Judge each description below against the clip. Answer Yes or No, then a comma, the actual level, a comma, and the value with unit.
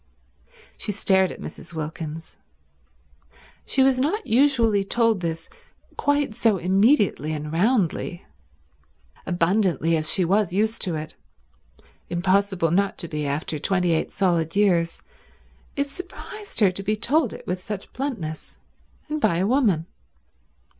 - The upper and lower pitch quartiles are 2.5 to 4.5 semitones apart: No, wide, 5.4 semitones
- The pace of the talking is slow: Yes, slow, 130 wpm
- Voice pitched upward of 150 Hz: Yes, high, 190 Hz